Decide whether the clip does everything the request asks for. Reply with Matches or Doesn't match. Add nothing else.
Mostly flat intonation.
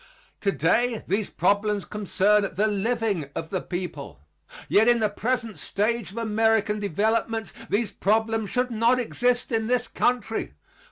Matches